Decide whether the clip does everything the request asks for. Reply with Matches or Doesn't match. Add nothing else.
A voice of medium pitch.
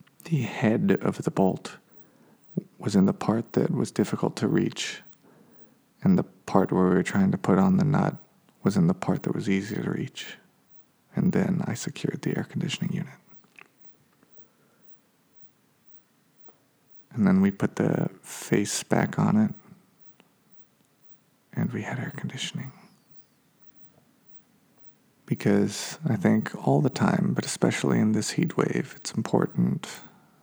Matches